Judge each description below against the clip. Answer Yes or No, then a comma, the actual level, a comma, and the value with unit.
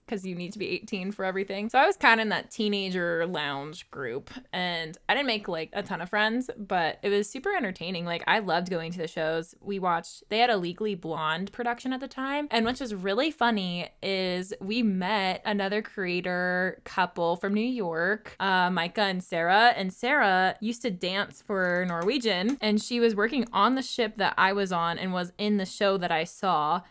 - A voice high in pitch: Yes, high, 195 Hz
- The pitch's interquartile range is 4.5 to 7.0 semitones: No, average, 3.8 semitones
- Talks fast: Yes, fast, 210 wpm